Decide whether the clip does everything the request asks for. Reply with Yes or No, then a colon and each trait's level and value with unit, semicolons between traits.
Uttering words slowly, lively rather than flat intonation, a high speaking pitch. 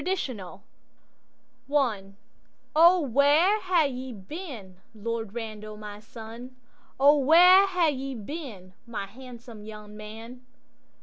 Yes: slow, 105 wpm; wide, 5.8 semitones; high, 245 Hz